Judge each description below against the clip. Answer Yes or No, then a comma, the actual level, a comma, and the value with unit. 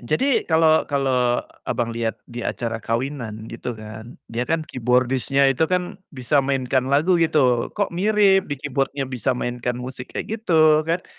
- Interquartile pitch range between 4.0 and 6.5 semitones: Yes, average, 4.6 semitones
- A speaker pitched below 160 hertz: Yes, low, 135 Hz